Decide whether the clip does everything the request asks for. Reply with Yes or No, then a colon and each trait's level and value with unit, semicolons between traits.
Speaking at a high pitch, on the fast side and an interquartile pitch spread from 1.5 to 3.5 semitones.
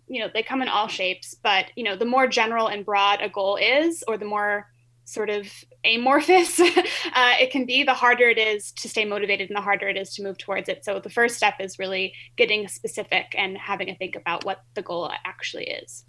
No: high, 210 Hz; fast, 230 wpm; average, 4.2 semitones